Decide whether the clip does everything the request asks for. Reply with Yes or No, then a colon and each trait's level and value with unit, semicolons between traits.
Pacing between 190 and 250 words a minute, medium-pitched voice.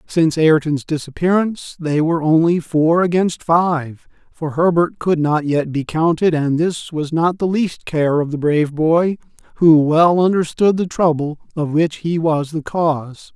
No: average, 170 wpm; medium, 160 Hz